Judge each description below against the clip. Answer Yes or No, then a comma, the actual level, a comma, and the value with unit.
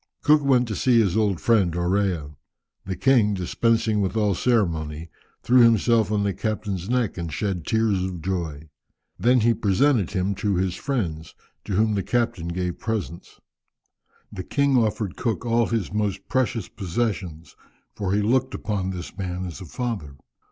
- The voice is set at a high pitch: No, low, 100 Hz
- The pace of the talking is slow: No, average, 165 wpm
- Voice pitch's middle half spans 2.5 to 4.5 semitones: Yes, average, 4.2 semitones